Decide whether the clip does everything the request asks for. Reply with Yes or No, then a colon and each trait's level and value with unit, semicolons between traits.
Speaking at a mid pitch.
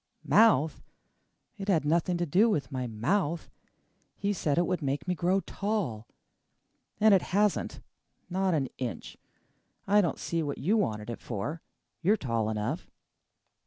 Yes: medium, 170 Hz